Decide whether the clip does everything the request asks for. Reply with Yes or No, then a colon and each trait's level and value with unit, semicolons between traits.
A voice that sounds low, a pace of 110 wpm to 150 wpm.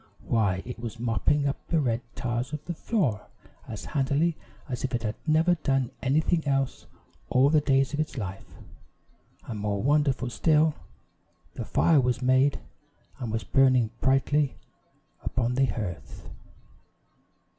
Yes: low, 130 Hz; average, 145 wpm